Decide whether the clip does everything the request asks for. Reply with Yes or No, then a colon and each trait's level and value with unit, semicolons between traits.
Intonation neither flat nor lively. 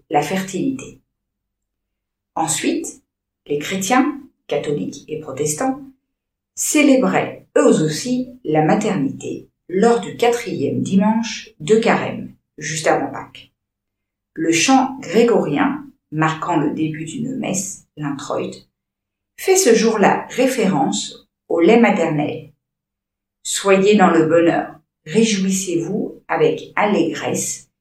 No: wide, 8.4 semitones